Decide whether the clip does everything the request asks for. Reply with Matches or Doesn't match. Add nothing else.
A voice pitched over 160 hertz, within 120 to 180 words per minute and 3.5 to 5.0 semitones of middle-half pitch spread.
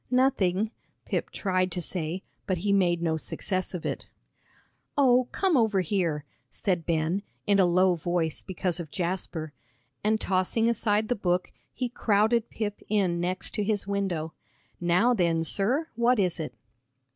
Matches